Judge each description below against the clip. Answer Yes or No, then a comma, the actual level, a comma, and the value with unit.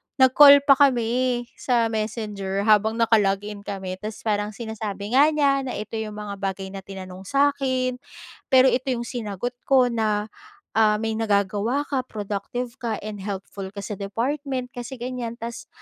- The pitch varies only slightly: No, average, 3.8 semitones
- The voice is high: Yes, high, 225 Hz